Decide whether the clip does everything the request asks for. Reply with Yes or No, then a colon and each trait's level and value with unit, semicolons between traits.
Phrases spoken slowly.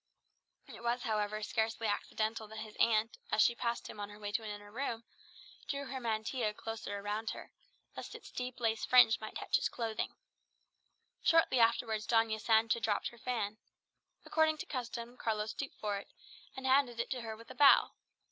No: average, 185 wpm